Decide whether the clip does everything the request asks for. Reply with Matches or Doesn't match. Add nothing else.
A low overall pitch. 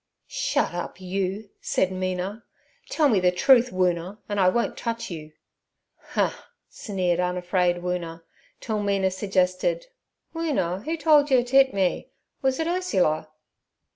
Doesn't match